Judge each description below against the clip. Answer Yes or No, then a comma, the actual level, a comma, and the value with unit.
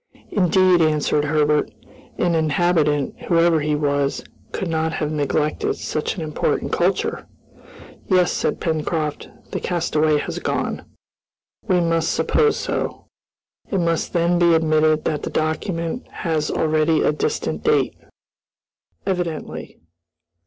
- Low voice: No, medium, 160 Hz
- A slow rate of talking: Yes, slow, 120 wpm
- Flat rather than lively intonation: Yes, narrow, 2.2 semitones